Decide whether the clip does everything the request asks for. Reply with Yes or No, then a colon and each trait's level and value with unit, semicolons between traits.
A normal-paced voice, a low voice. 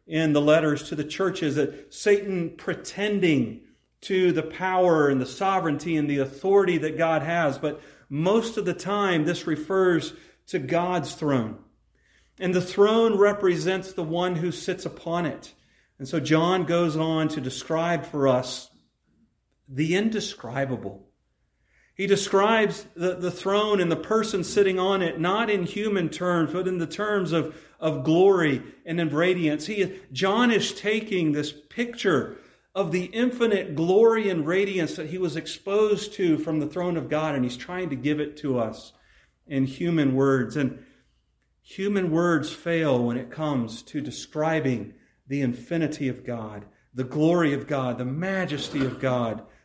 No: average, 160 wpm; medium, 165 Hz